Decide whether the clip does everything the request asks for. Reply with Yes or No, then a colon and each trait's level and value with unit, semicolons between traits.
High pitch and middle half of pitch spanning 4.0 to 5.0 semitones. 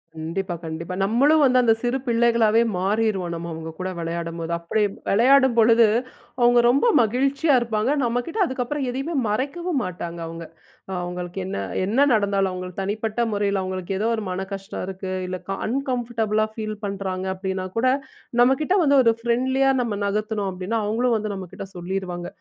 Yes: high, 215 Hz; average, 4.6 semitones